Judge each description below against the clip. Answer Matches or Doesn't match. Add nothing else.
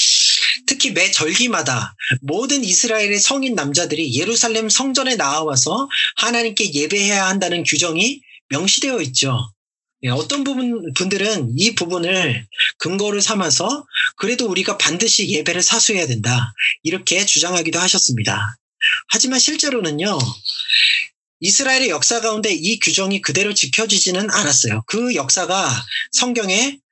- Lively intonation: Matches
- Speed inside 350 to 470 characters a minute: Doesn't match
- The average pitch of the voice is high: Matches